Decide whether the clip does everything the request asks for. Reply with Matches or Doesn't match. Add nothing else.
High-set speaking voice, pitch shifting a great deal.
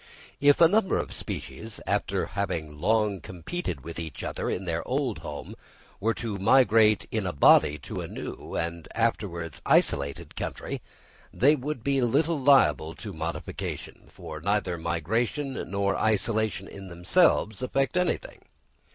Doesn't match